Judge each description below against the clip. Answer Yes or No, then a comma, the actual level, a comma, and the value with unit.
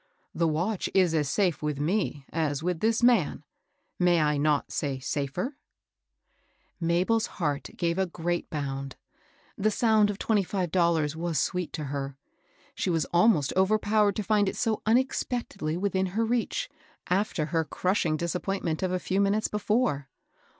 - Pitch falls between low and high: Yes, medium, 180 Hz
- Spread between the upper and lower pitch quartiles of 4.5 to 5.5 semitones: Yes, average, 5.0 semitones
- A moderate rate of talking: Yes, average, 165 wpm